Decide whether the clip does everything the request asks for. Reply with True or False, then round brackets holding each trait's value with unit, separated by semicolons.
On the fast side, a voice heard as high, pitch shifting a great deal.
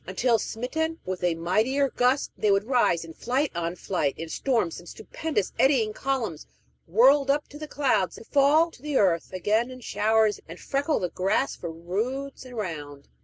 False (175 wpm; 225 Hz; 7.3 semitones)